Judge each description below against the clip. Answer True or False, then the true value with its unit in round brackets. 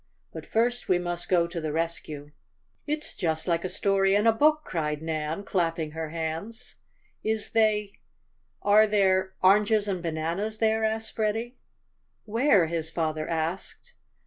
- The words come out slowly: False (145 wpm)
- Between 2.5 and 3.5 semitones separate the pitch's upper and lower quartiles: False (5.0 semitones)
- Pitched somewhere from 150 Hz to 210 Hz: True (190 Hz)